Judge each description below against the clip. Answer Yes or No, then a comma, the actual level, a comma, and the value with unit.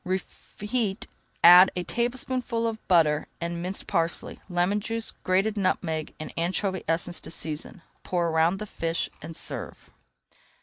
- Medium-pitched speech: Yes, medium, 180 Hz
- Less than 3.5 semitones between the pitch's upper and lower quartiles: No, average, 3.8 semitones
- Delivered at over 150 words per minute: No, slow, 135 wpm